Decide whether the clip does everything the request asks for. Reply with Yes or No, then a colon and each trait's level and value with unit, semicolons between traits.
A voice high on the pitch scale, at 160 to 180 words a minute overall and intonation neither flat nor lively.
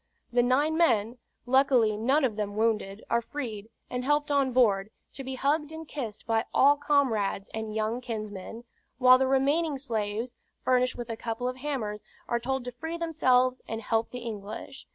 Yes: very high, 250 Hz; average, 175 wpm; average, 3.6 semitones